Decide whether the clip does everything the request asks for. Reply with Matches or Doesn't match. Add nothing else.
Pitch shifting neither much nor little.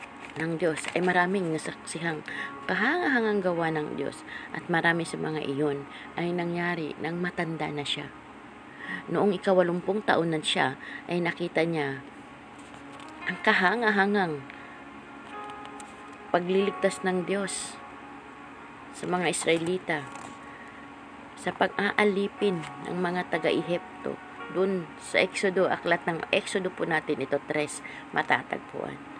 Matches